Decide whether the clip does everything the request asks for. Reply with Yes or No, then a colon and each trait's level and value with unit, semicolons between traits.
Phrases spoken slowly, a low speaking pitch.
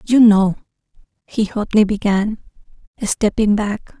No: slow, 105 wpm; high, 210 Hz